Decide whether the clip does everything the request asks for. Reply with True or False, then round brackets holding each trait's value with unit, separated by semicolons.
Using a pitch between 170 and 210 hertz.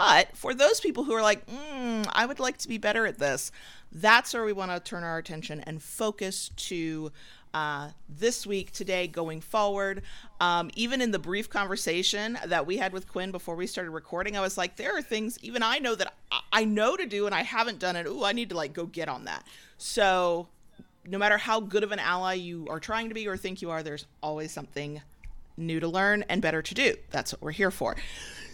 True (190 Hz)